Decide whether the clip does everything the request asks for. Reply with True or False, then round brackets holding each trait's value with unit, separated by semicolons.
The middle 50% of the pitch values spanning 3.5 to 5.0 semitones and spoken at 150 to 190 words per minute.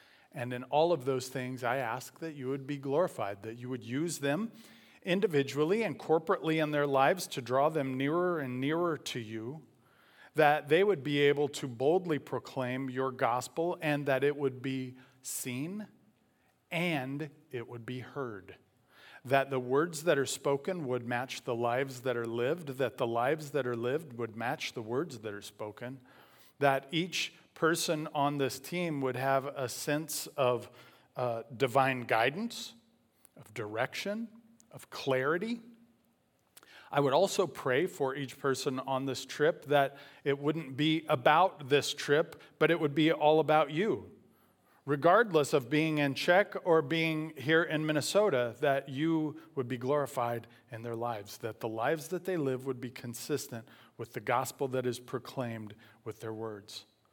True (3.8 semitones; 165 wpm)